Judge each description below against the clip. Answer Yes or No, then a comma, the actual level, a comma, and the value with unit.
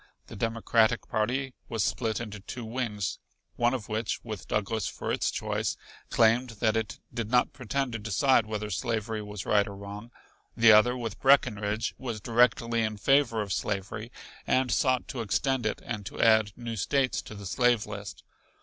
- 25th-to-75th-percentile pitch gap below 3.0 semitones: Yes, narrow, 2.5 semitones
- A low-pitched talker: Yes, low, 110 Hz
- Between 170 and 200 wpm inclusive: Yes, average, 175 wpm